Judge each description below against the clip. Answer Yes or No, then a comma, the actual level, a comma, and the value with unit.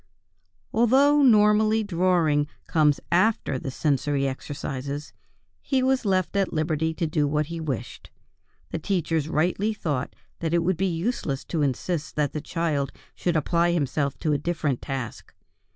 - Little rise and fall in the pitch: No, average, 4.3 semitones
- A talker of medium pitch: Yes, medium, 160 Hz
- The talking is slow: No, average, 150 wpm